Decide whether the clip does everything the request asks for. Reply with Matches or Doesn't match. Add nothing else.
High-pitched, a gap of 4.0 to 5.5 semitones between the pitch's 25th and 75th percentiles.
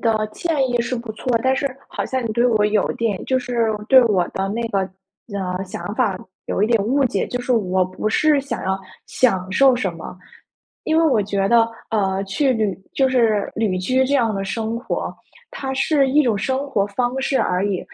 Matches